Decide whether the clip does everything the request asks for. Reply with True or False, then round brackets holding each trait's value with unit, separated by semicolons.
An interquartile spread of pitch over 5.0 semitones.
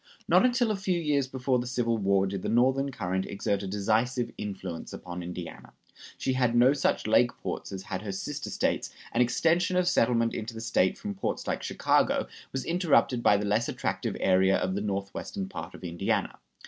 True (5.5 semitones)